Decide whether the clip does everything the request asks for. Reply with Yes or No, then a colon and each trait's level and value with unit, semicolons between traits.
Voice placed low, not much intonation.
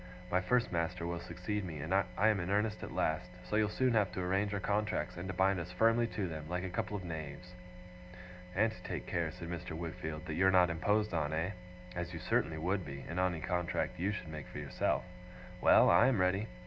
No: very low, 90 Hz; average, 3.4 semitones